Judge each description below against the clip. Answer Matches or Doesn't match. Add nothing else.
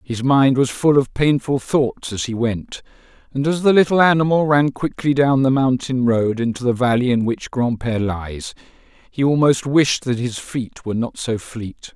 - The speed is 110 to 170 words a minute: Doesn't match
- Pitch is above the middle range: Doesn't match